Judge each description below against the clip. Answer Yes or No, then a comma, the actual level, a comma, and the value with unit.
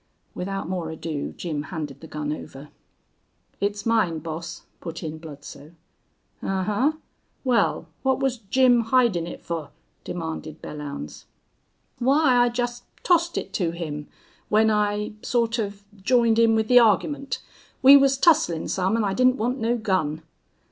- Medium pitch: No, high, 205 Hz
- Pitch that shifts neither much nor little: No, wide, 7.0 semitones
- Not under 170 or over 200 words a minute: No, average, 145 wpm